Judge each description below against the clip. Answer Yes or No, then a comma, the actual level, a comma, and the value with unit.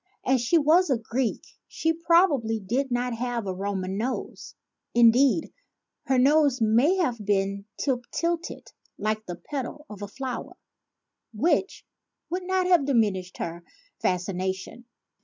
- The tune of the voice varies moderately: No, wide, 6.4 semitones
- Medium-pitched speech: No, high, 245 Hz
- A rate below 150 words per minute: Yes, average, 140 wpm